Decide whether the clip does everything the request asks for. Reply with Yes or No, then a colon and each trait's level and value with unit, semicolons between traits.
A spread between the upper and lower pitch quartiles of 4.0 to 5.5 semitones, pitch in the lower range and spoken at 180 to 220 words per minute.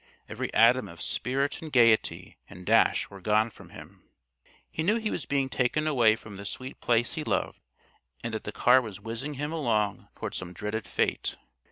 Yes: average, 4.7 semitones; low, 120 Hz; average, 190 wpm